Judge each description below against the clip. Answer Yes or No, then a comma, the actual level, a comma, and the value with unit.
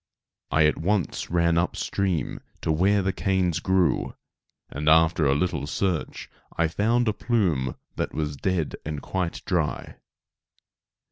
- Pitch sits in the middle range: No, very low, 85 Hz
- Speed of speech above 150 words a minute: No, average, 140 wpm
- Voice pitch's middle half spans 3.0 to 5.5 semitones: Yes, average, 3.7 semitones